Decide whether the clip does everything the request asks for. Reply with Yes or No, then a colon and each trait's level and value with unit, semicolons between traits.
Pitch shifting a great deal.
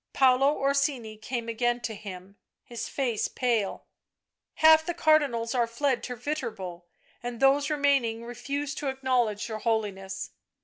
No: average, 3.9 semitones